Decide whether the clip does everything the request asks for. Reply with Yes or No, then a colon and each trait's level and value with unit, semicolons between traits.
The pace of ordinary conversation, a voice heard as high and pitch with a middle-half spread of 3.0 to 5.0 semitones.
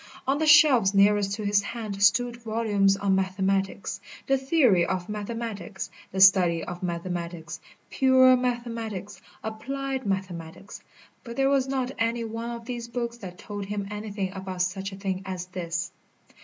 Yes: average, 155 wpm; high, 205 Hz; average, 3.8 semitones